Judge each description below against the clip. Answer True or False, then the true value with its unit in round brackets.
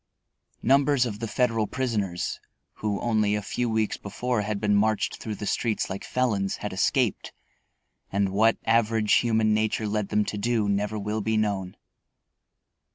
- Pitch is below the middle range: True (110 Hz)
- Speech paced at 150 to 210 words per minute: True (160 wpm)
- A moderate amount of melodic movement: False (1.9 semitones)